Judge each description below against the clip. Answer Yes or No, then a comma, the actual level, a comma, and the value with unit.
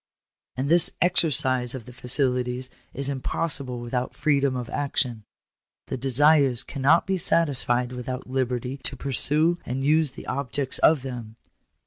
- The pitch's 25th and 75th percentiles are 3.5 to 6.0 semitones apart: No, narrow, 2.4 semitones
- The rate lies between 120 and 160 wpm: Yes, slow, 135 wpm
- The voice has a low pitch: Yes, low, 130 Hz